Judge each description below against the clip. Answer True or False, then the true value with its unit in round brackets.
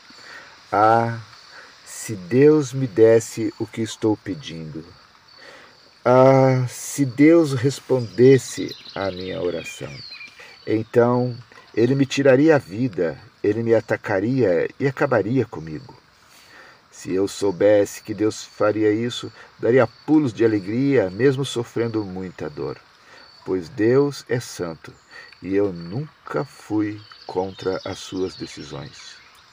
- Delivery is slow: True (110 wpm)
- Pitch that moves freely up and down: False (4.6 semitones)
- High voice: False (115 Hz)